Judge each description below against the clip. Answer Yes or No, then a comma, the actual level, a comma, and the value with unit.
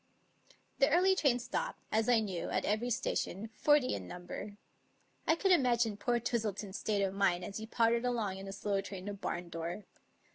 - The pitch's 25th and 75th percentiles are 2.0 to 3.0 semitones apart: No, average, 3.8 semitones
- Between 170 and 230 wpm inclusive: Yes, average, 180 wpm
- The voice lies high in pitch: Yes, high, 215 Hz